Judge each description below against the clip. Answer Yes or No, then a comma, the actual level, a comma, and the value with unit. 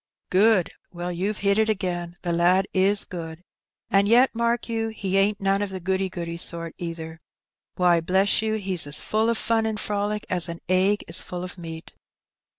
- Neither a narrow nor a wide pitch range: Yes, average, 3.4 semitones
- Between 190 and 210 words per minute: Yes, average, 195 wpm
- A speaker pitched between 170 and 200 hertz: Yes, high, 190 Hz